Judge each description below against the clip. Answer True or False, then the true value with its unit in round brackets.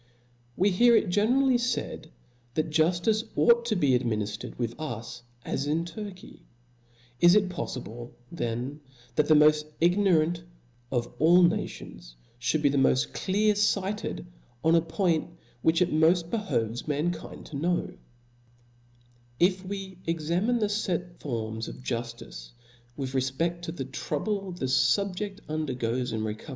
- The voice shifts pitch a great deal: True (6.6 semitones)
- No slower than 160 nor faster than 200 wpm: False (150 wpm)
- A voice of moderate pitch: True (160 Hz)